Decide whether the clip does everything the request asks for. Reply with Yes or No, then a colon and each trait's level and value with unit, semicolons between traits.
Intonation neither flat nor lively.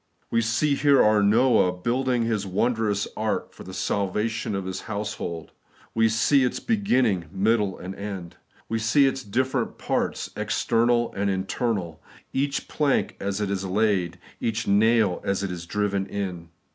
Yes: average, 3.4 semitones